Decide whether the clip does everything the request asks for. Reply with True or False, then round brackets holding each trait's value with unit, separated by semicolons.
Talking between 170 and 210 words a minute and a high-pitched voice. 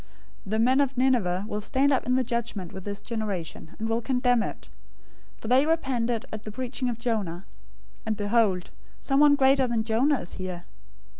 True (180 wpm; 235 Hz)